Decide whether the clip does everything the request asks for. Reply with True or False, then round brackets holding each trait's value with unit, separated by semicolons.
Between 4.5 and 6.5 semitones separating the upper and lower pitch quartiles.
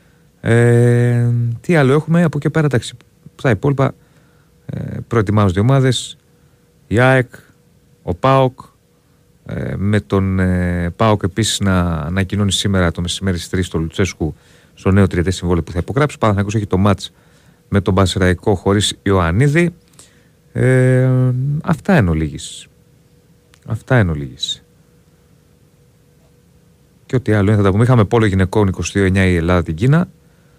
True (5.6 semitones)